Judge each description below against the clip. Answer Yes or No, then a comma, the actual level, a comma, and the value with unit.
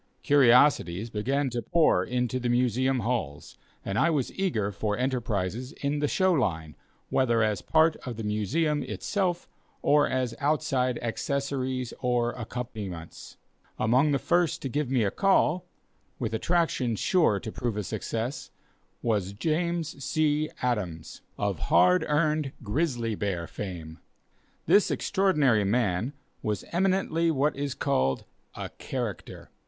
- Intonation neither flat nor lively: No, wide, 5.7 semitones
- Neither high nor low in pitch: No, low, 125 Hz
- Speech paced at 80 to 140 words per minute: Yes, slow, 135 wpm